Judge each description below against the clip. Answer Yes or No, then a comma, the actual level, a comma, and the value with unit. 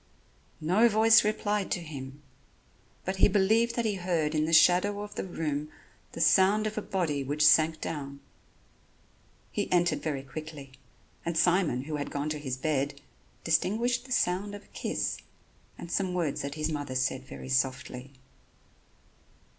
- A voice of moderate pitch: Yes, medium, 160 Hz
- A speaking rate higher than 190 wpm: No, average, 160 wpm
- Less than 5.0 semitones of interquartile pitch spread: No, average, 5.3 semitones